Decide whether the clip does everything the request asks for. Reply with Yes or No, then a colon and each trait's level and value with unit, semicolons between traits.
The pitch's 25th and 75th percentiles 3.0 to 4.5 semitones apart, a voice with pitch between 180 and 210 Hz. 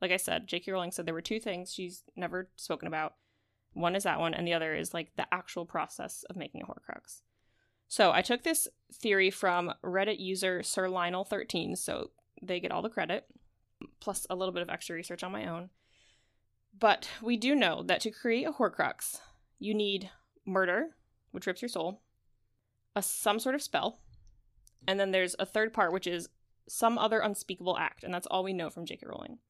Yes: average, 4.1 semitones; medium, 185 Hz